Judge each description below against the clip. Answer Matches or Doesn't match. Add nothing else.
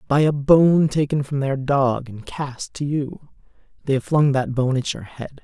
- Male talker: Matches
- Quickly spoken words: Matches